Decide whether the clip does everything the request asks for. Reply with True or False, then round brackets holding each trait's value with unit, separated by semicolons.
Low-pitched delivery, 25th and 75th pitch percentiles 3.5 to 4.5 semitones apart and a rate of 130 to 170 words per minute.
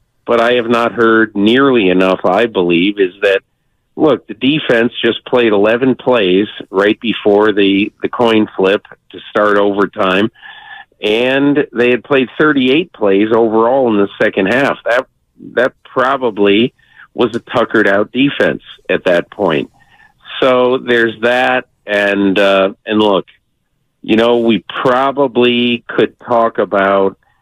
True (115 Hz; 3.8 semitones; 140 wpm)